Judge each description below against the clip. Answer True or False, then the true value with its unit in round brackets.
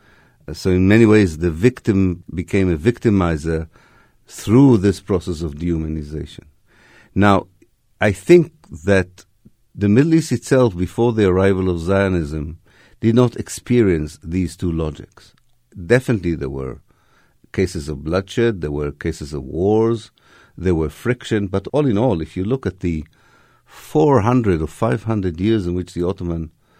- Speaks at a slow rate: False (145 wpm)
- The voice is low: True (95 Hz)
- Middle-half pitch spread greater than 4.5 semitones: True (5.4 semitones)